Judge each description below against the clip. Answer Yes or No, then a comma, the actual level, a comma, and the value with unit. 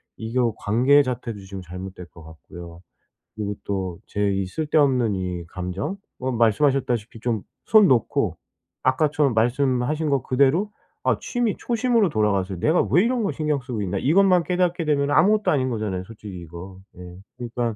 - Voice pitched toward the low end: Yes, low, 120 Hz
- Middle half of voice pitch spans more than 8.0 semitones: No, wide, 7.6 semitones